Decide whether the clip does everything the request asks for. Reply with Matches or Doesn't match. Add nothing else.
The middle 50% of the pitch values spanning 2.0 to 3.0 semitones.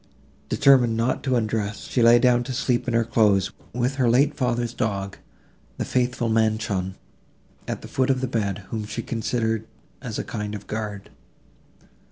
Matches